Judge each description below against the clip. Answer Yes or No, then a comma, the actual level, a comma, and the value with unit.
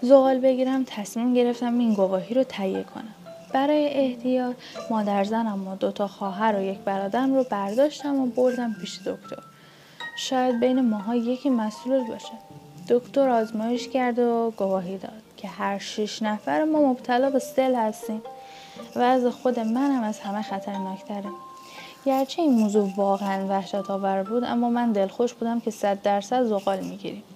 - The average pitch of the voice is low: No, high, 230 Hz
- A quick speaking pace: Yes, fast, 160 wpm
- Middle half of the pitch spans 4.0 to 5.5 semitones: Yes, average, 4.4 semitones